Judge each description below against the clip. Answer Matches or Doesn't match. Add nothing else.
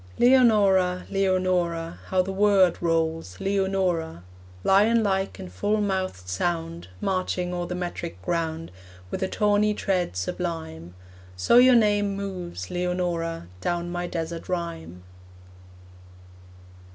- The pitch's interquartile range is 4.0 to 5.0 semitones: Doesn't match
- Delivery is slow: Matches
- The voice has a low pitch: Doesn't match